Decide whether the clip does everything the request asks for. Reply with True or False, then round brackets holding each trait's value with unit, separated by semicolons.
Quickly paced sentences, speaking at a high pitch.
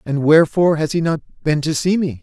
False (245 wpm; 160 Hz)